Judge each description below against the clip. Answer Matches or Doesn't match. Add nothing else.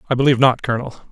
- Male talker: Matches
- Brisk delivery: Matches